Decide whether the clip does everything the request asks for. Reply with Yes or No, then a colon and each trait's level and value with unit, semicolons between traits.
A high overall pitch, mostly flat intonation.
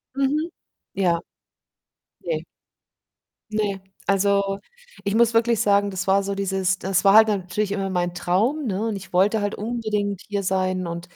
Yes: high, 200 Hz; narrow, 2.2 semitones